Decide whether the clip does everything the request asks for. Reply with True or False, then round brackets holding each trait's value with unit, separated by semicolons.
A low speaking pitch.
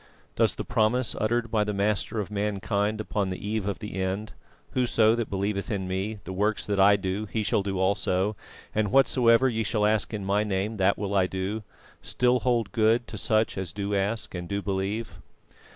True (105 Hz)